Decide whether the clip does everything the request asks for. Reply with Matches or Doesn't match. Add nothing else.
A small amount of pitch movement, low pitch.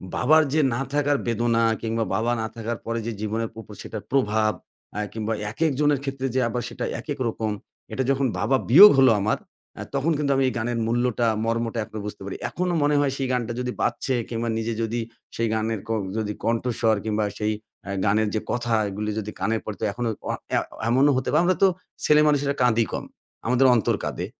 Doesn't match